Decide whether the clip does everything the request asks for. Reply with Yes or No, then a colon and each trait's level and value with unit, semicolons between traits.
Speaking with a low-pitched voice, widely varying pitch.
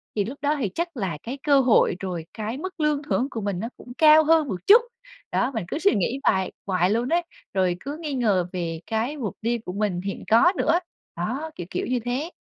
No: high, 235 Hz; wide, 7.4 semitones